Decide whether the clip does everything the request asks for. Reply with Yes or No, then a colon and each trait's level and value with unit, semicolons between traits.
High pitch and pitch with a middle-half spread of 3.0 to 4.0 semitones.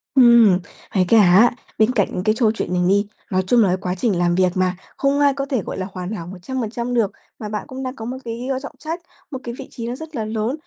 No: high, 225 Hz; average, 5.3 semitones